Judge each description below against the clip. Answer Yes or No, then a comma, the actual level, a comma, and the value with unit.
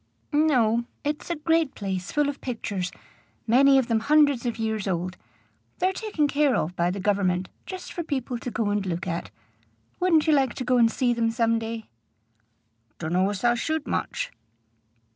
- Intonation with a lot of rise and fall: Yes, wide, 6.2 semitones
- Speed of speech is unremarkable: Yes, average, 180 wpm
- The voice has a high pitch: Yes, high, 235 Hz